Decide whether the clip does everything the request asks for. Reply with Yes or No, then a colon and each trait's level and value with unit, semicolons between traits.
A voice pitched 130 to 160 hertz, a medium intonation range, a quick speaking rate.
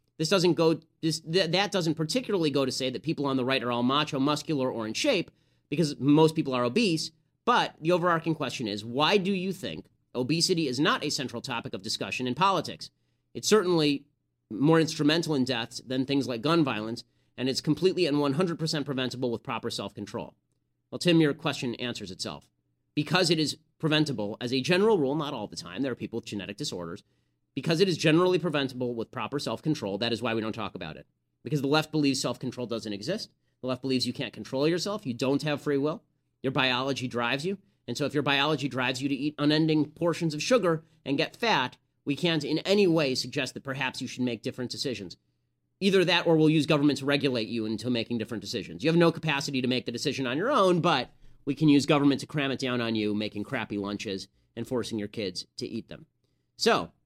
Yes: medium, 140 Hz; average, 4.8 semitones; fast, 220 wpm